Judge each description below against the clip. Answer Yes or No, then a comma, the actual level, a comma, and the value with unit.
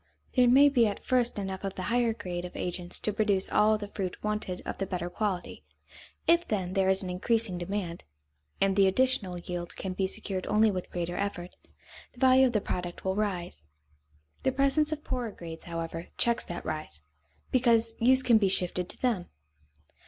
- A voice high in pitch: Yes, high, 195 Hz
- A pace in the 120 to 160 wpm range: No, average, 190 wpm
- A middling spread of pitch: Yes, average, 4.5 semitones